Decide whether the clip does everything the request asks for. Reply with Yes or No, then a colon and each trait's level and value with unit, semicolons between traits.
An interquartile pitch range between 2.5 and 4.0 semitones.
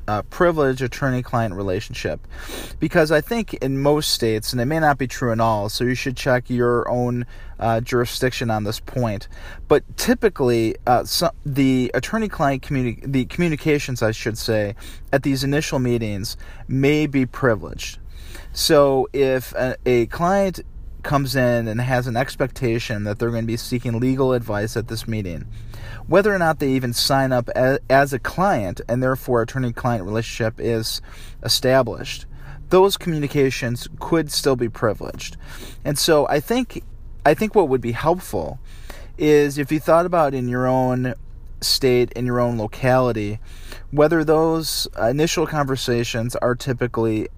Yes: average, 3.7 semitones